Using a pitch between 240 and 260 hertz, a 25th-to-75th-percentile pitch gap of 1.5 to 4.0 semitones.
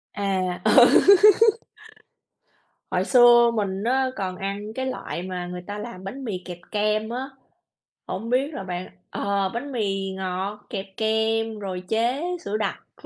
No: high, 210 Hz; average, 3.7 semitones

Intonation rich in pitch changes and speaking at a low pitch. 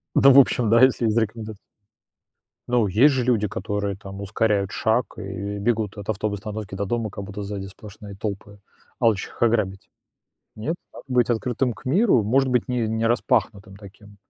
No: average, 2.9 semitones; low, 110 Hz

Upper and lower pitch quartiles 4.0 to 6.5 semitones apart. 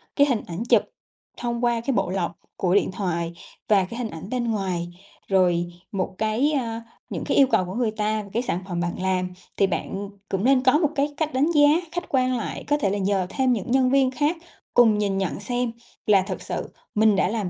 Yes: average, 5.1 semitones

